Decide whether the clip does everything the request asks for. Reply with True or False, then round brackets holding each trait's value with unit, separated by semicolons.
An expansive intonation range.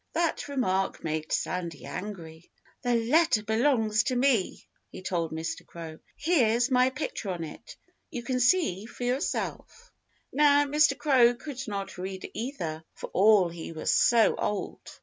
True (6.5 semitones)